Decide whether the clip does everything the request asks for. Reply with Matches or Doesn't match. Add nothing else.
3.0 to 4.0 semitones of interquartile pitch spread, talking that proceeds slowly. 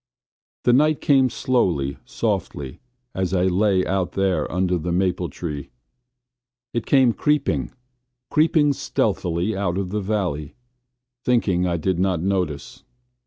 Doesn't match